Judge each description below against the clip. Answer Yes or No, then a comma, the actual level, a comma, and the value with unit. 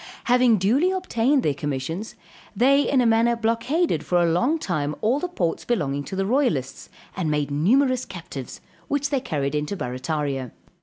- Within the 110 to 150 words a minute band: No, average, 165 wpm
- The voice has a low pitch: No, high, 205 Hz